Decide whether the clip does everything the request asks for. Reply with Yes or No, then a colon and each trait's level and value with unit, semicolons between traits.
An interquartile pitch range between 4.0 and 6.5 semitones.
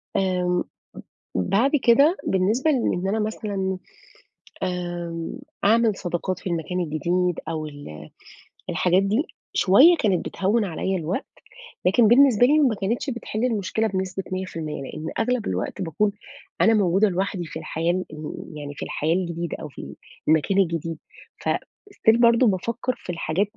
Yes: average, 4.4 semitones